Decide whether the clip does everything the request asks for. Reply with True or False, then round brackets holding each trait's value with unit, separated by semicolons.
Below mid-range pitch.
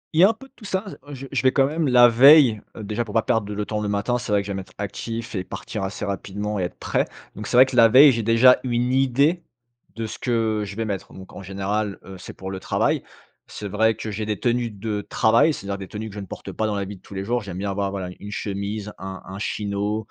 True (105 Hz)